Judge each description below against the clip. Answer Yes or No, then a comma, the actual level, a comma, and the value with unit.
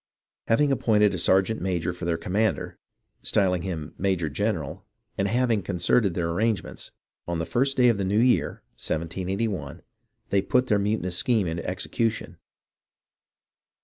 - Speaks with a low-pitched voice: Yes, low, 100 Hz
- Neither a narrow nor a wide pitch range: Yes, average, 4.2 semitones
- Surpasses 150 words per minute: No, average, 145 wpm